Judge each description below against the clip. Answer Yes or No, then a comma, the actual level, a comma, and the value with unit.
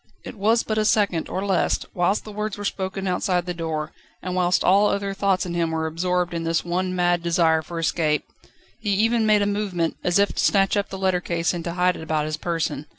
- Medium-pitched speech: Yes, medium, 180 Hz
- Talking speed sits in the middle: No, fast, 235 wpm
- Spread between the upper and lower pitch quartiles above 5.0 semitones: No, average, 2.9 semitones